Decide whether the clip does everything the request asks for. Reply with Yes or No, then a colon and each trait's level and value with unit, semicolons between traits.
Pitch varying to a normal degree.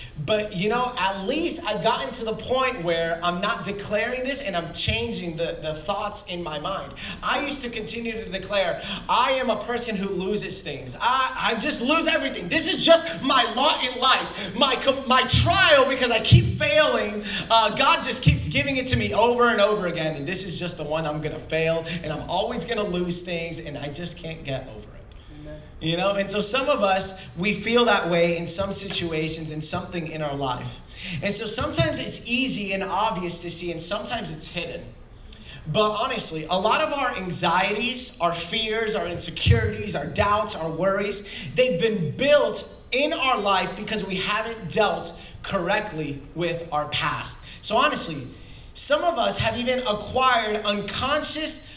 No: wide, 6.1 semitones